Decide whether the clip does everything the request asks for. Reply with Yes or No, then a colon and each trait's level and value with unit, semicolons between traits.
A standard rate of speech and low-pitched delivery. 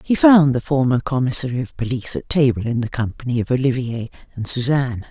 Yes: average, 190 wpm; low, 130 Hz